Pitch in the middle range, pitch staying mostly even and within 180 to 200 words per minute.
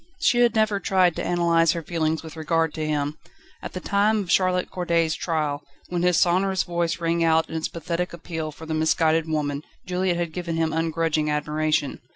Yes: medium, 165 Hz; narrow, 2.2 semitones; average, 195 wpm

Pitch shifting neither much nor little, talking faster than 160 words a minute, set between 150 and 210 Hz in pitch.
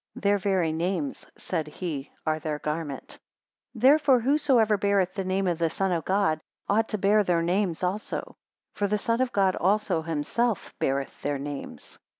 Yes: average, 4.6 semitones; average, 170 wpm; high, 190 Hz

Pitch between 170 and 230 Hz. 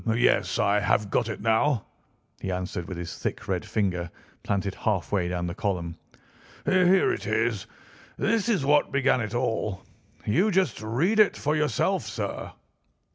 No: low, 110 Hz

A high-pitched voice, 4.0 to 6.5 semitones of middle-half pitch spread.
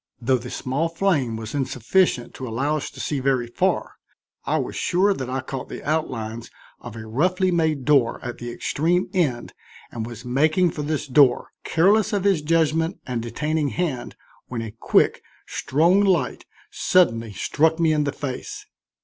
No: medium, 145 Hz; average, 5.3 semitones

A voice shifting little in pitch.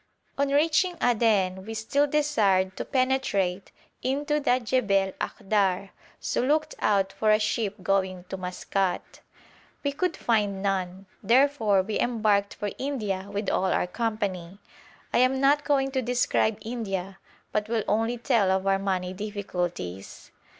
No: average, 4.9 semitones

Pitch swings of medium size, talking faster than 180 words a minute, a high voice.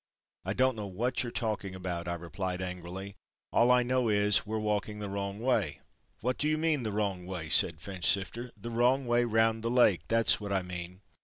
No: average, 4.2 semitones; average, 200 wpm; low, 105 Hz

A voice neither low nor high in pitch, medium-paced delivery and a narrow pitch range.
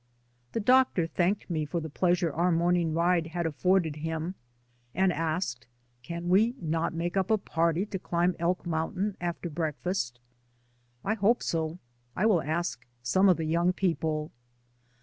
Yes: medium, 170 Hz; average, 155 wpm; narrow, 2.3 semitones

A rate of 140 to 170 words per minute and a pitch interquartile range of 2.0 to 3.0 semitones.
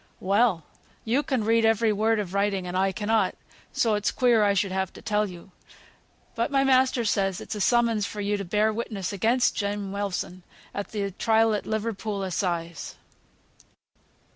Yes: average, 165 wpm; narrow, 2.5 semitones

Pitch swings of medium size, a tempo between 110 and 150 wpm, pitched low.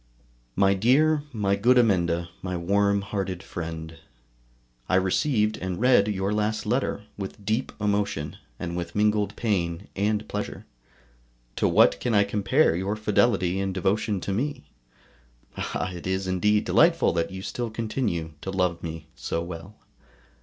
Yes: average, 3.1 semitones; average, 145 wpm; low, 100 Hz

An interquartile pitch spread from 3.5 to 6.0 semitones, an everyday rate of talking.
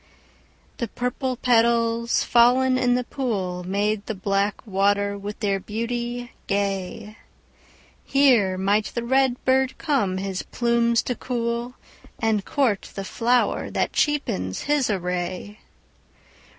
No: average, 3.8 semitones; slow, 110 wpm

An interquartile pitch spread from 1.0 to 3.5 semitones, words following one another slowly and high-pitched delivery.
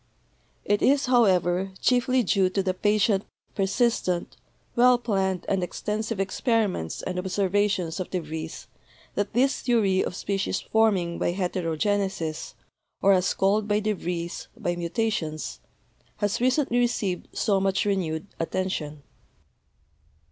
Yes: average, 3.2 semitones; slow, 125 wpm; high, 195 Hz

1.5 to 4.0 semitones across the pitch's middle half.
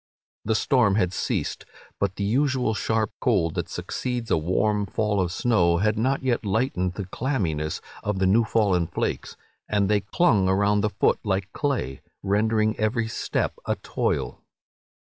Yes: average, 3.1 semitones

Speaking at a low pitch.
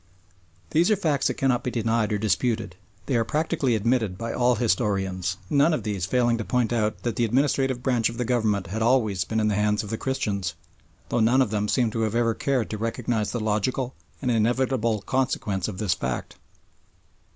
Yes: low, 115 Hz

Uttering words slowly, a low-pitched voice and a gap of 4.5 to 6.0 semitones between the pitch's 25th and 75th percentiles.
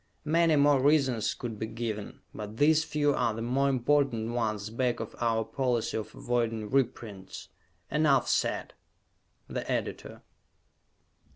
No: slow, 130 wpm; low, 120 Hz; average, 3.9 semitones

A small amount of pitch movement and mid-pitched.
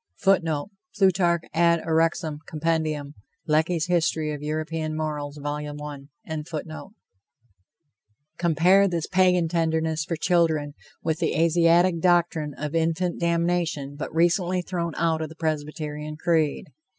Yes: narrow, 2.1 semitones; medium, 160 Hz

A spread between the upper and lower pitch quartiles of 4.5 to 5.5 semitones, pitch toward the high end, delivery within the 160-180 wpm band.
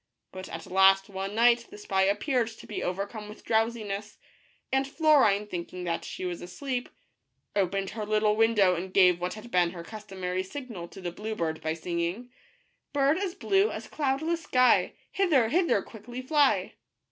Yes: average, 5.1 semitones; high, 210 Hz; average, 175 wpm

